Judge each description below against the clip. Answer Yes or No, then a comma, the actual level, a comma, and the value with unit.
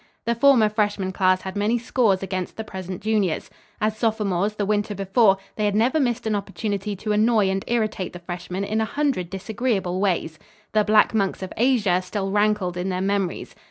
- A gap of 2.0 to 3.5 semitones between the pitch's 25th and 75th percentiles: Yes, narrow, 2.6 semitones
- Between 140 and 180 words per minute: No, average, 190 wpm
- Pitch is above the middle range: Yes, high, 205 Hz